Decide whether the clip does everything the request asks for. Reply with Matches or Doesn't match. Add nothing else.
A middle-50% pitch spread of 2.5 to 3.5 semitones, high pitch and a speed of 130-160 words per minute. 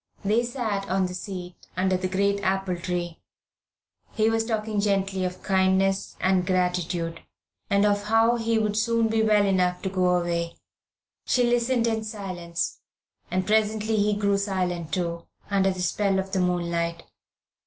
Matches